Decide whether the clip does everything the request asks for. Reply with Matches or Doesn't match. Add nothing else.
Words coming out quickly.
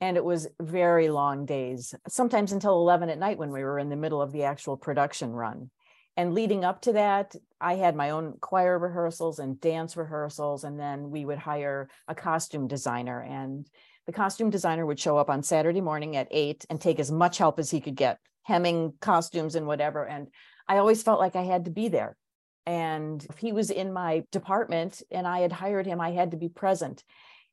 Matches